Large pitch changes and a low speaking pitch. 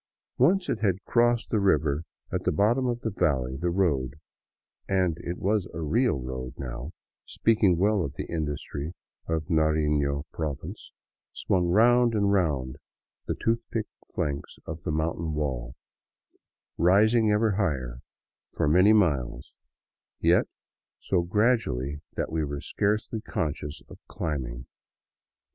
Yes: wide, 6.5 semitones; very low, 85 Hz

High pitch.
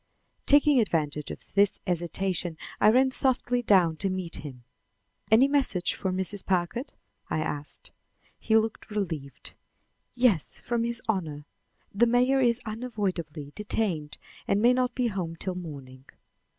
Yes: high, 195 Hz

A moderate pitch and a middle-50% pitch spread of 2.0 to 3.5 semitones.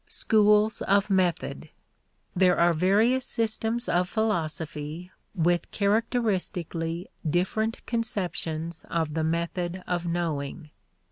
No: medium, 180 Hz; average, 4.2 semitones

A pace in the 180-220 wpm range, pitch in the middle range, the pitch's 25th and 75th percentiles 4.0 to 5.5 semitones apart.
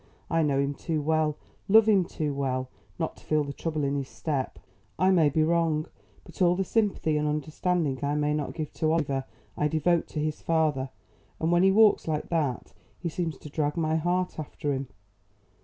No: average, 200 wpm; medium, 155 Hz; narrow, 2.6 semitones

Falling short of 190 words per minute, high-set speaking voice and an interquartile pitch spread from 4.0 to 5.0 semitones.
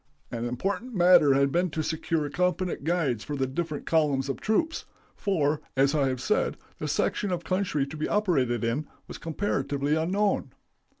No: average, 170 wpm; medium, 155 Hz; average, 4.7 semitones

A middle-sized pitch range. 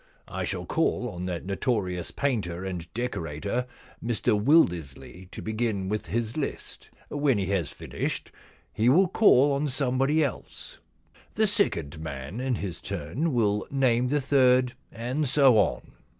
No: wide, 6.5 semitones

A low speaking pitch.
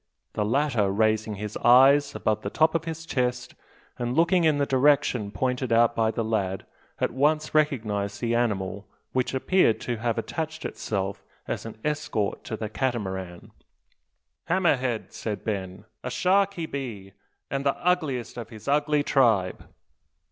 Yes: low, 120 Hz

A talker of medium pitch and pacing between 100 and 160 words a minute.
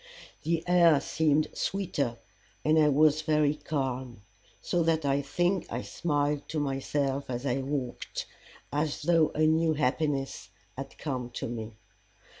Yes: medium, 145 Hz; average, 140 wpm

